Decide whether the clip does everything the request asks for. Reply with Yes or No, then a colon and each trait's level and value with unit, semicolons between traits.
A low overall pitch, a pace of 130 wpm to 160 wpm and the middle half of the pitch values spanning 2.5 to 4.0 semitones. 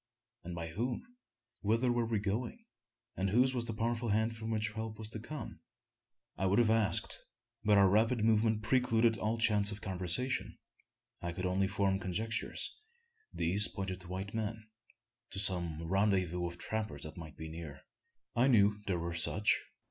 No: low, 105 Hz; average, 170 wpm; average, 3.4 semitones